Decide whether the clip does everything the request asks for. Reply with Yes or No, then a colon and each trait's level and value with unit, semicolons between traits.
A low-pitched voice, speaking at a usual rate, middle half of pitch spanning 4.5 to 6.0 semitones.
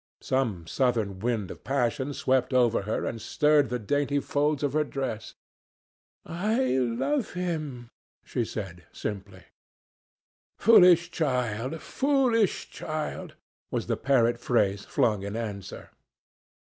No: low, 130 Hz; slow, 120 wpm; wide, 5.5 semitones